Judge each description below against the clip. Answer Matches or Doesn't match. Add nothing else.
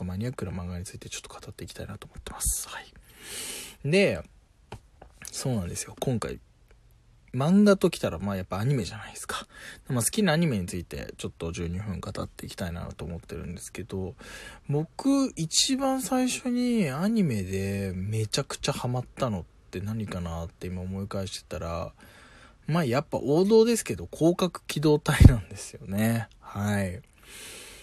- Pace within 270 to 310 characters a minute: Doesn't match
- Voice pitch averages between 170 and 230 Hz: Doesn't match